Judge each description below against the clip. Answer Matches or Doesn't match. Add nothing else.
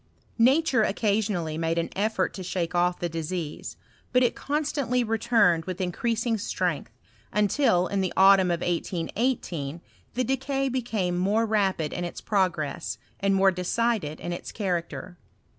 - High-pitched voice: Matches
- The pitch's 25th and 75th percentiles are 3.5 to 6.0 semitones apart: Matches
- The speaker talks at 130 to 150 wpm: Matches